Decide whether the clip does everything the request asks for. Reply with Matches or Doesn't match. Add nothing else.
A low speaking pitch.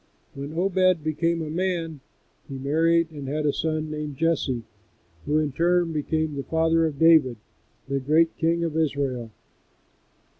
Doesn't match